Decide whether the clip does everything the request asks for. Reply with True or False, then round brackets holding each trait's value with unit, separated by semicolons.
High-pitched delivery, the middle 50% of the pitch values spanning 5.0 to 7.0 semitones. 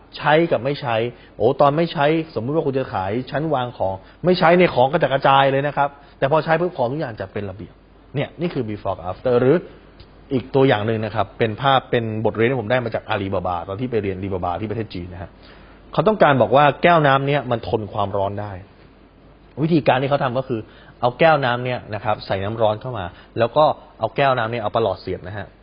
False (120 Hz; 5.6 semitones)